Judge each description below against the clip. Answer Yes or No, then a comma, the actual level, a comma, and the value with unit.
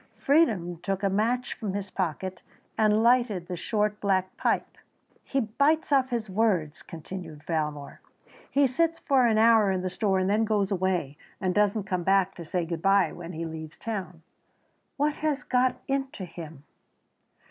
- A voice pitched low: No, high, 195 Hz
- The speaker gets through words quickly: No, average, 170 wpm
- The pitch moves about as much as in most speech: Yes, average, 4.5 semitones